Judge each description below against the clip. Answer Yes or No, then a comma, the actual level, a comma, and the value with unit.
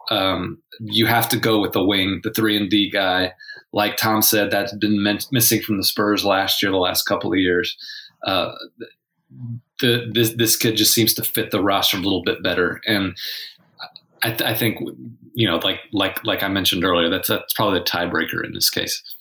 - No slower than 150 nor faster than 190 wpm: No, fast, 205 wpm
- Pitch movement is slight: Yes, narrow, 2.3 semitones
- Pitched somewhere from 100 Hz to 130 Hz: Yes, low, 110 Hz